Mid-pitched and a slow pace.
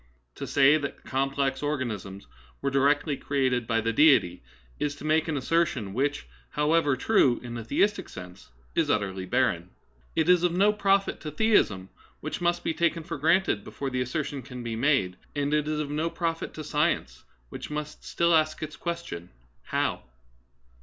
No: medium, 145 Hz; average, 175 wpm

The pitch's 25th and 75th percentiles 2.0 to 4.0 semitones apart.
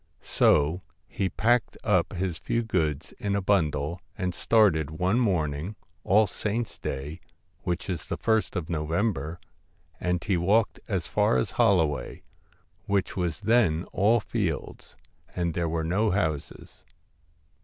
No: average, 4.5 semitones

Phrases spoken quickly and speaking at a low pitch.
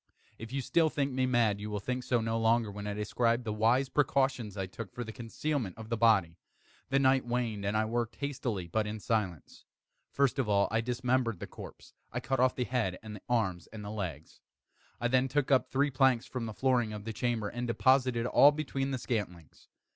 Yes: fast, 215 wpm; low, 115 Hz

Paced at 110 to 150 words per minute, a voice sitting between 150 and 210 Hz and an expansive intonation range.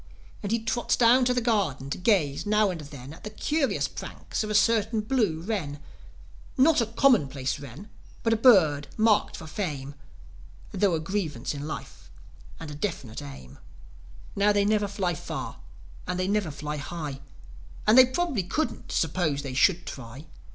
No: average, 165 wpm; high, 190 Hz; wide, 7.0 semitones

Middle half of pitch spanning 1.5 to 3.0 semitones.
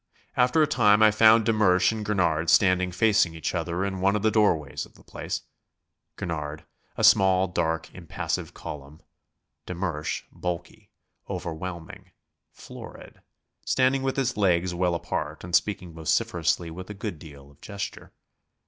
No: average, 4.1 semitones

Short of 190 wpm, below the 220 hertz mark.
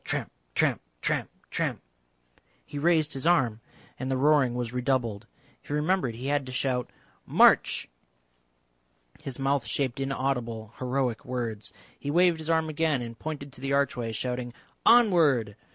Yes: average, 145 wpm; low, 135 Hz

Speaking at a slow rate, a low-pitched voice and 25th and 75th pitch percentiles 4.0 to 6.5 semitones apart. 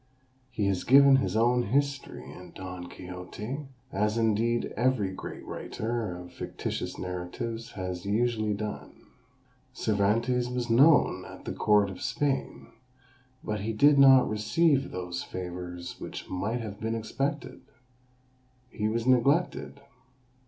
Yes: slow, 125 wpm; low, 110 Hz; average, 4.7 semitones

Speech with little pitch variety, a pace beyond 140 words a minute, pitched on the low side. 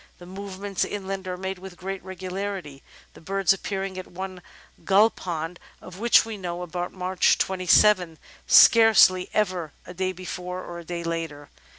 No: narrow, 1.6 semitones; average, 165 wpm; medium, 185 Hz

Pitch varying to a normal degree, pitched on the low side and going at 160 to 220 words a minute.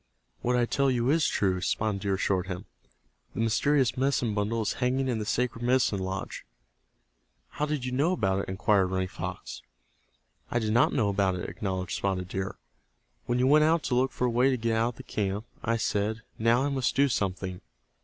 Yes: average, 4.6 semitones; low, 115 Hz; fast, 205 wpm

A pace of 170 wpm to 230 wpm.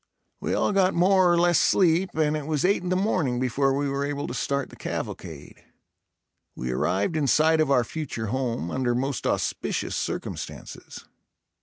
Yes: average, 175 wpm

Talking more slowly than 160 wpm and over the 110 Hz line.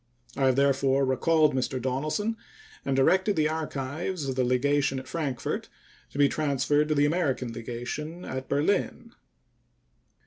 Yes: average, 140 wpm; medium, 140 Hz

